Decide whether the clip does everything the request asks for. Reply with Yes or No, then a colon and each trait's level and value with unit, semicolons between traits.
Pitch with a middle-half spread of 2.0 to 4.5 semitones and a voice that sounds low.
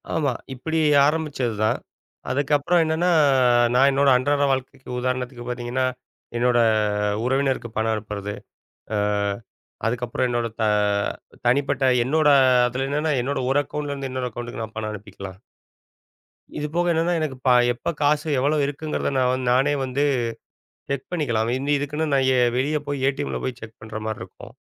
Yes: average, 3.3 semitones; low, 130 Hz